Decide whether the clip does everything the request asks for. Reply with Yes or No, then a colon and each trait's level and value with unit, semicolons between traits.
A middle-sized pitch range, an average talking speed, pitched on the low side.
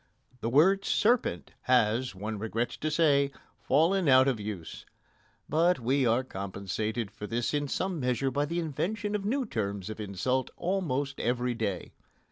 No: wide, 6.5 semitones; average, 155 wpm; low, 130 Hz